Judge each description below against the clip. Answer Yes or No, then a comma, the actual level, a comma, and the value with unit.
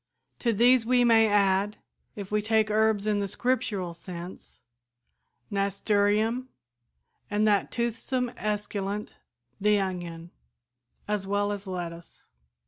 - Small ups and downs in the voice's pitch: Yes, narrow, 2.2 semitones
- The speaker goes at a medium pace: No, slow, 115 wpm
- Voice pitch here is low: No, high, 205 Hz